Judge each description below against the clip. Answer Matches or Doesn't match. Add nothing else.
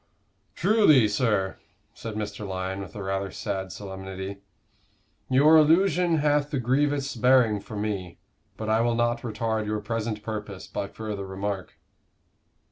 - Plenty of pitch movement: Doesn't match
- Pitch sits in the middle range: Doesn't match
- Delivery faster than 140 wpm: Doesn't match